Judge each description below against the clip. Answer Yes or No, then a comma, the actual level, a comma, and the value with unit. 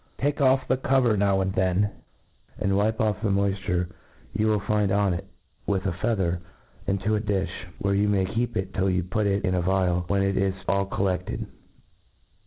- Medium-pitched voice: No, low, 100 Hz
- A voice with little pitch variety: Yes, narrow, 2.0 semitones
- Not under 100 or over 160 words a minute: No, average, 195 wpm